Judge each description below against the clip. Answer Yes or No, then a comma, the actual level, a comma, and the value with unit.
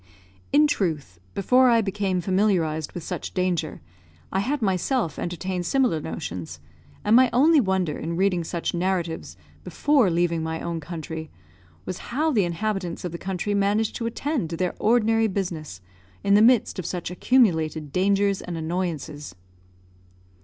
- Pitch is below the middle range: No, medium, 185 Hz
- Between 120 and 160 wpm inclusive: Yes, average, 150 wpm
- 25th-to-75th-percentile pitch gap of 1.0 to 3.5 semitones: No, average, 4.6 semitones